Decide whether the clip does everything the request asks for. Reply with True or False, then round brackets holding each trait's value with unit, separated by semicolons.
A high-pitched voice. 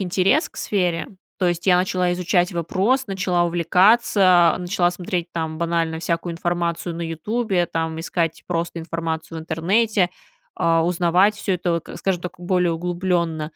False (175 Hz)